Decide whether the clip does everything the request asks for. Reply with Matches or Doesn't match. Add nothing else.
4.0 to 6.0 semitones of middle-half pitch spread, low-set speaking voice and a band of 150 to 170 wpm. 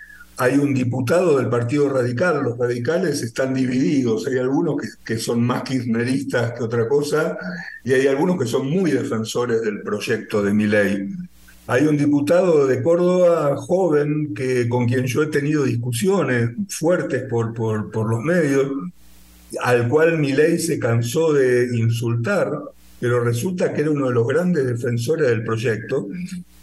Matches